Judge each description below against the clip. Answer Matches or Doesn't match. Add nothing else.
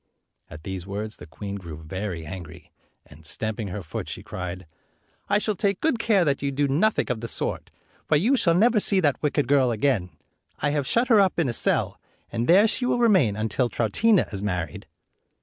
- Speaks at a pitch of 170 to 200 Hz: Doesn't match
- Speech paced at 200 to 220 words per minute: Matches